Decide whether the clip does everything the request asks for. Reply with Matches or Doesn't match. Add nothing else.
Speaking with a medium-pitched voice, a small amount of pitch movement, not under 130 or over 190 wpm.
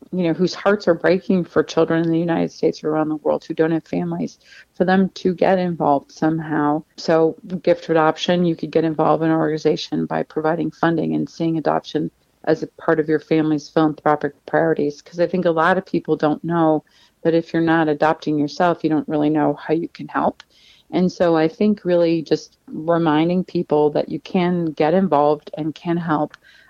Doesn't match